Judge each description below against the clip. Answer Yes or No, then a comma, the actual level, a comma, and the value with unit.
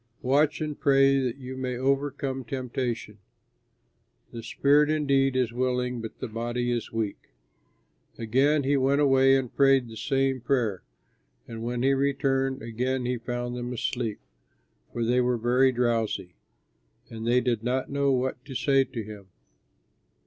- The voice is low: Yes, low, 125 Hz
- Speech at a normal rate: Yes, average, 150 wpm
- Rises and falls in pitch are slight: Yes, narrow, 2.3 semitones